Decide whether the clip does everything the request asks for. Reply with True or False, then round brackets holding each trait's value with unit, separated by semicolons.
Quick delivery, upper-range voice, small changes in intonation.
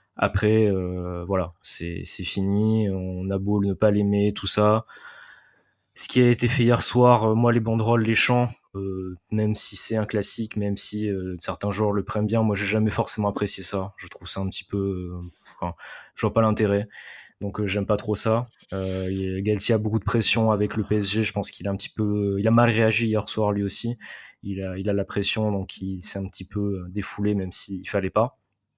False (225 wpm; 105 Hz; 2.1 semitones)